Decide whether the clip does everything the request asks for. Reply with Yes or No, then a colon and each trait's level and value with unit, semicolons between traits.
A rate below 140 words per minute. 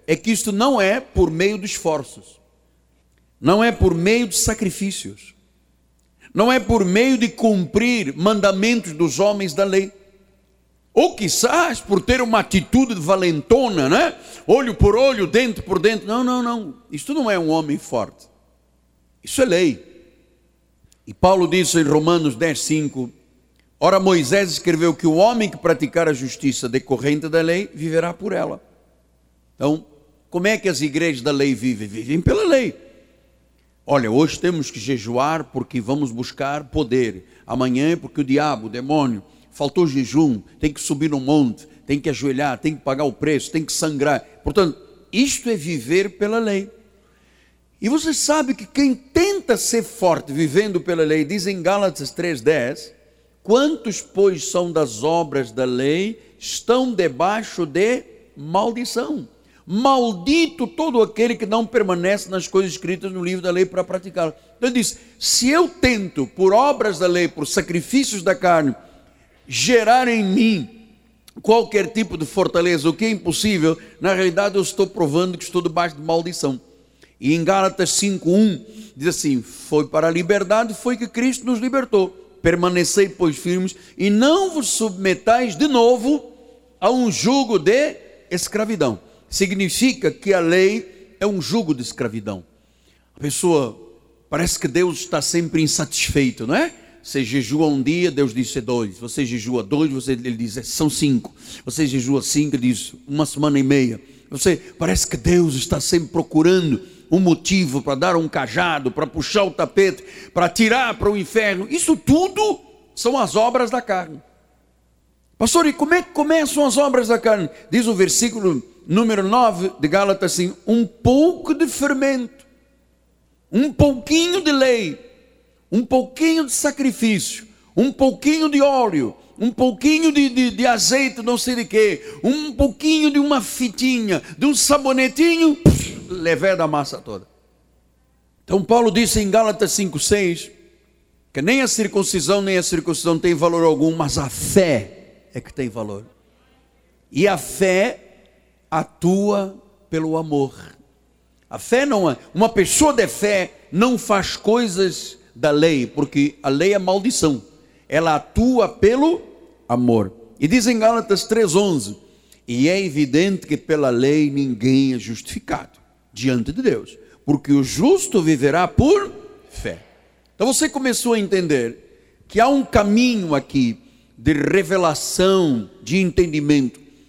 No: average, 155 wpm